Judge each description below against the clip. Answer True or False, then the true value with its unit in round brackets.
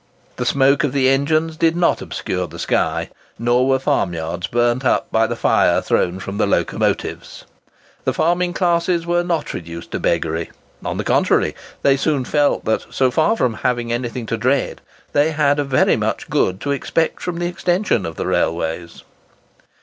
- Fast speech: False (170 wpm)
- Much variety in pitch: True (6.3 semitones)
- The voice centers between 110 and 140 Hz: True (135 Hz)